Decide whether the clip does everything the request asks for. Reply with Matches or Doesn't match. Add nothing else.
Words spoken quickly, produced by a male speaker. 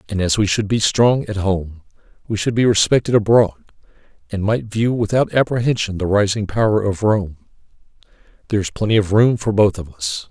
Doesn't match